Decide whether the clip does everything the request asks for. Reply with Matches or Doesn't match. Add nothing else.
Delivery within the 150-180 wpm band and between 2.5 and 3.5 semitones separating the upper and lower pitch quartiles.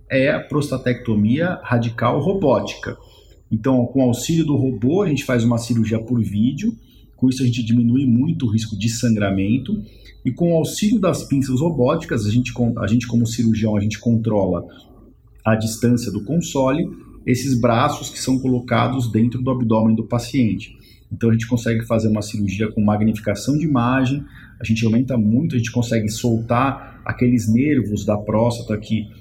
Matches